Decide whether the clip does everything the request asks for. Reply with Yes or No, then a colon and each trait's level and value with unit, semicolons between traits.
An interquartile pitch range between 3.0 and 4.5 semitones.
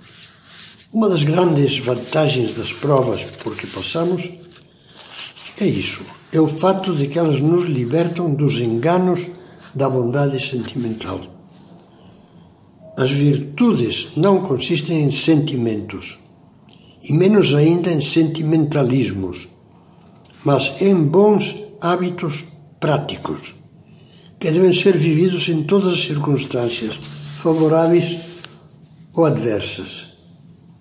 Yes: average, 4.2 semitones